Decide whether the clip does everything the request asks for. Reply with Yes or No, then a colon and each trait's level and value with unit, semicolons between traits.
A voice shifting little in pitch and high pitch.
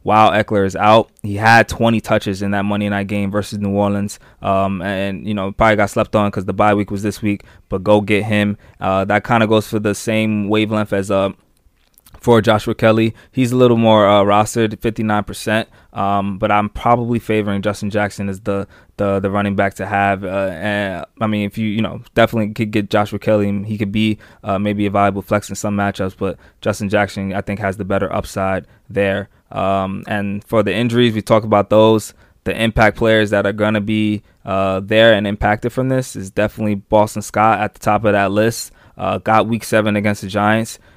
No: narrow, 1.5 semitones; low, 105 Hz